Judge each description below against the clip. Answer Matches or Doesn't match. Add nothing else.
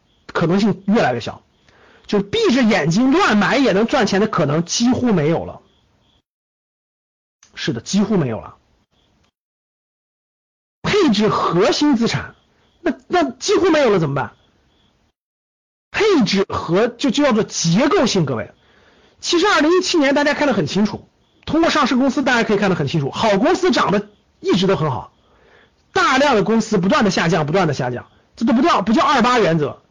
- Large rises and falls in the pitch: Matches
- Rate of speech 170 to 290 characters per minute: Matches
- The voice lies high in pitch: Matches